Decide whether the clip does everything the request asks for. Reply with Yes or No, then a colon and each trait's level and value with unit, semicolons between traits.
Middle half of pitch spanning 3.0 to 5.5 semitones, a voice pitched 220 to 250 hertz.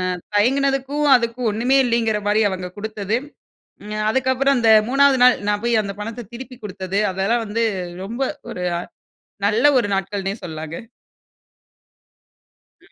Yes: average, 3.6 semitones; high, 225 Hz